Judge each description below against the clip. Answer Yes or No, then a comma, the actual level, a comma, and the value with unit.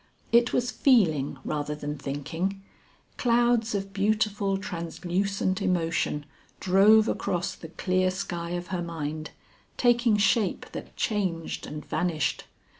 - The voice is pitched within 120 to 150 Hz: No, medium, 185 Hz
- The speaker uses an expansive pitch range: No, average, 4.1 semitones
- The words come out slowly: Yes, slow, 115 wpm